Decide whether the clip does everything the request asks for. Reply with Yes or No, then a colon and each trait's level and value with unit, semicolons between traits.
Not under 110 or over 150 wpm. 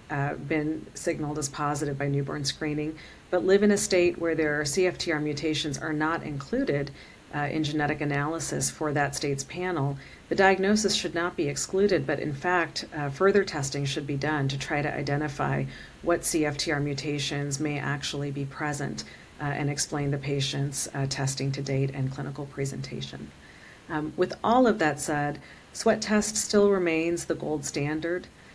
No: average, 165 wpm